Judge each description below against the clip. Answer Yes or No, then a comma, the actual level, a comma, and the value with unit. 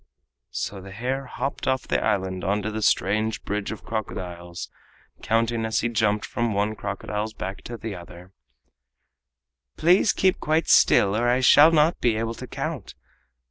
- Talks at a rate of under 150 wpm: No, average, 165 wpm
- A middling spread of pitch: Yes, average, 3.4 semitones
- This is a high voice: No, low, 110 Hz